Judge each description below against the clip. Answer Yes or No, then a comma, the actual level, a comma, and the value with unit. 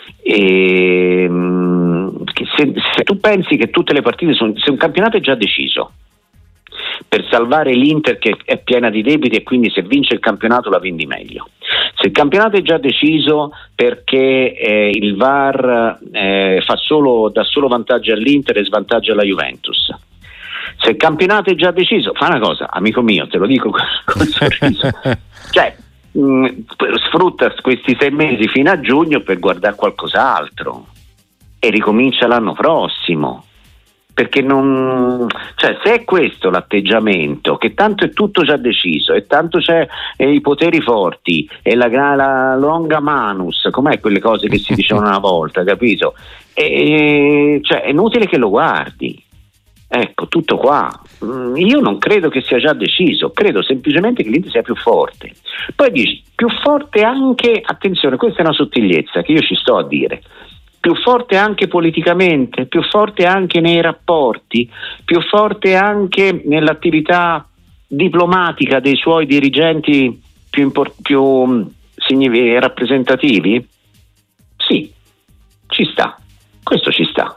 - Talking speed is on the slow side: No, average, 145 wpm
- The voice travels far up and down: Yes, wide, 8.0 semitones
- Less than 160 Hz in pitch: Yes, medium, 140 Hz